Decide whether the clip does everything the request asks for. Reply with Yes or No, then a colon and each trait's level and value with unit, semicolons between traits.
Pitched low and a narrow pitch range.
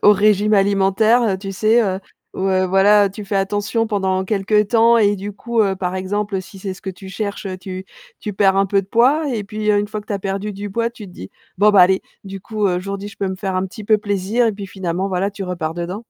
No: high, 200 Hz; narrow, 1.8 semitones